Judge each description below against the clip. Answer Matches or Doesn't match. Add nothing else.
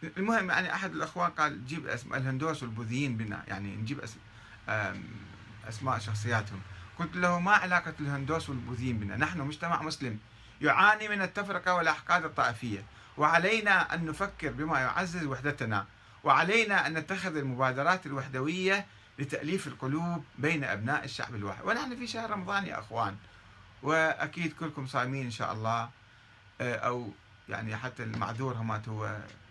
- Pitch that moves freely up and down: Matches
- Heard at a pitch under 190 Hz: Matches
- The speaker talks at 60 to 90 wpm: Doesn't match